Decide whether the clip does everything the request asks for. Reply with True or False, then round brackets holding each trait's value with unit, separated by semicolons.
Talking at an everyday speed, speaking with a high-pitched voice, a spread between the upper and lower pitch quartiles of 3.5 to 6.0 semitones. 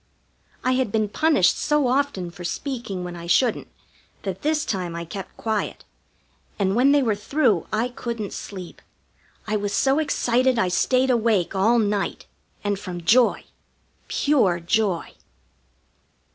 True (145 wpm; 215 Hz; 5.2 semitones)